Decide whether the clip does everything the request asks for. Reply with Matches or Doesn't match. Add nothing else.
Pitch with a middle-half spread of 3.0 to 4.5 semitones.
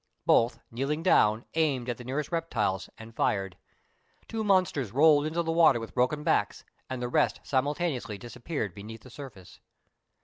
Doesn't match